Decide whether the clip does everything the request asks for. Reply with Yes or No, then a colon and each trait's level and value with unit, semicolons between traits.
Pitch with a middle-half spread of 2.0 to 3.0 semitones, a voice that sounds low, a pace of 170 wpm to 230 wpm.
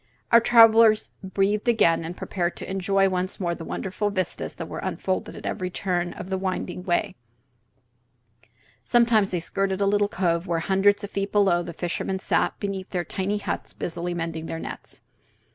No: narrow, 2.6 semitones; high, 190 Hz; average, 175 wpm